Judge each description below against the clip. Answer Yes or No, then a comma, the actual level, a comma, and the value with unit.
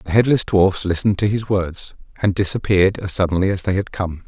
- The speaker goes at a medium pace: No, fast, 210 wpm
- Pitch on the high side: No, very low, 95 Hz